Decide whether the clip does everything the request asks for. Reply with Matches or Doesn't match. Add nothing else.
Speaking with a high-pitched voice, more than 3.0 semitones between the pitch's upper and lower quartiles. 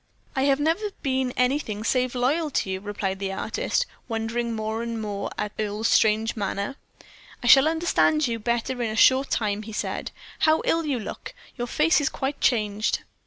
Matches